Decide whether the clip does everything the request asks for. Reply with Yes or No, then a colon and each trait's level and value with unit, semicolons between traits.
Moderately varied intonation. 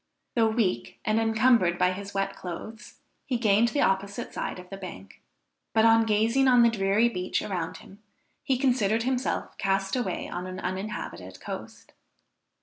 Yes: average, 3.7 semitones